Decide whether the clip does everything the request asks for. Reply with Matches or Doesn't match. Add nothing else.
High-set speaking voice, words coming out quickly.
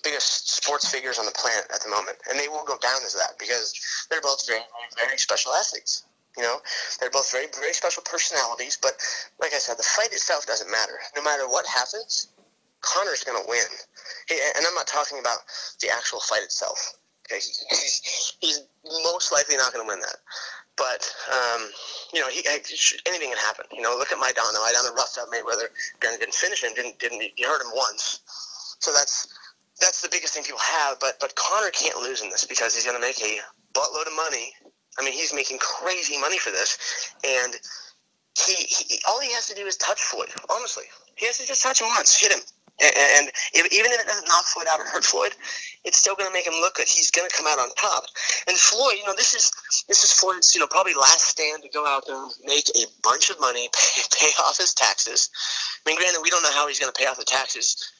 Matches